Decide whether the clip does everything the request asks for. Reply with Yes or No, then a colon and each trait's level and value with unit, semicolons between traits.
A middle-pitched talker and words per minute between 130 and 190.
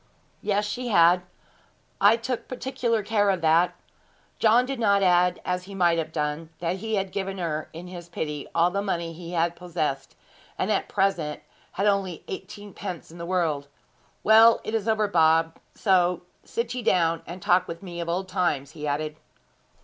Yes: medium, 180 Hz; average, 180 wpm